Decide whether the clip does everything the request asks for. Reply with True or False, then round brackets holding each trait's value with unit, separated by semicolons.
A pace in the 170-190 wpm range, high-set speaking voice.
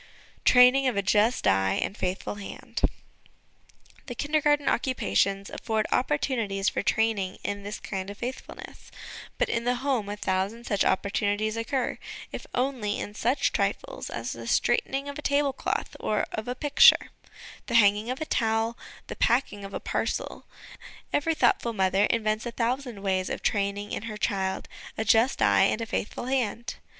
False (160 wpm; 225 Hz)